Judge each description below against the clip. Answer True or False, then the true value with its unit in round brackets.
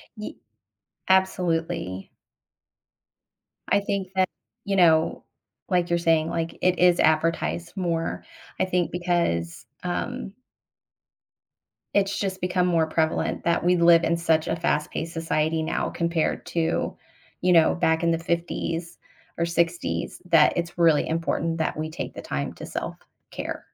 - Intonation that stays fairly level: True (1.7 semitones)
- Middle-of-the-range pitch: True (170 Hz)